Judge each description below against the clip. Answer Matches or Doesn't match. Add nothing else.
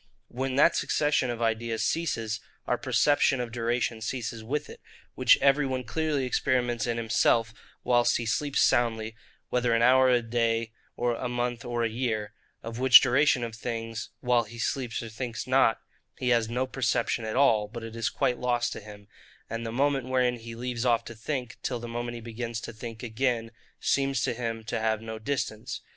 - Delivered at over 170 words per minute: Matches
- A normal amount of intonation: Doesn't match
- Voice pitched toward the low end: Matches